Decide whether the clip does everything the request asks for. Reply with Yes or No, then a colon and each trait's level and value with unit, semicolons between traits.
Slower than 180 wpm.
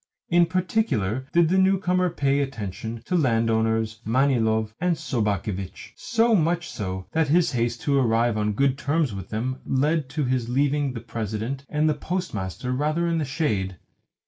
Yes: average, 160 wpm